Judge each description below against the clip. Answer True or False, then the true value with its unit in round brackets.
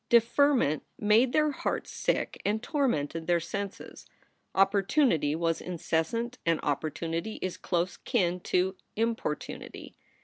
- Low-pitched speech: False (190 Hz)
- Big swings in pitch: True (5.9 semitones)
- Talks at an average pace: False (110 wpm)